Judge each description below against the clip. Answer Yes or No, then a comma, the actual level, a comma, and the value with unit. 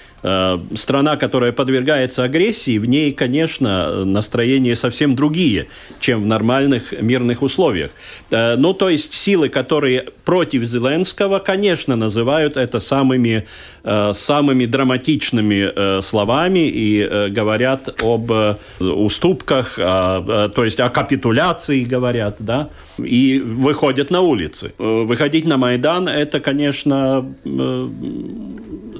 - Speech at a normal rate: No, slow, 100 wpm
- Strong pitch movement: No, average, 4.8 semitones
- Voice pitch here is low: Yes, low, 130 Hz